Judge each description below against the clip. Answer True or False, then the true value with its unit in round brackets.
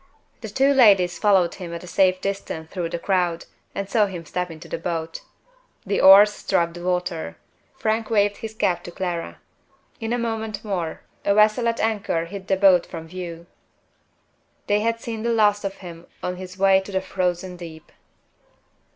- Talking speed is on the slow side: False (180 wpm)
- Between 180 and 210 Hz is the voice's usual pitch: True (190 Hz)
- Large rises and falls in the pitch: False (3.3 semitones)